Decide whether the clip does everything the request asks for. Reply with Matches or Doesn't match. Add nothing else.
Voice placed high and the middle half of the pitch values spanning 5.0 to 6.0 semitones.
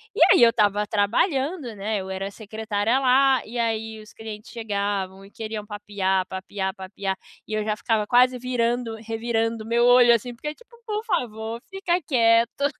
Doesn't match